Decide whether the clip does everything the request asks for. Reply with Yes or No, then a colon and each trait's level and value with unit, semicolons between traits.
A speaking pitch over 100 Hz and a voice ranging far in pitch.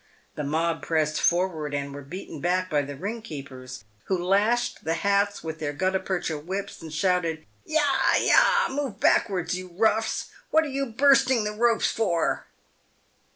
Yes: medium, 185 Hz; wide, 5.8 semitones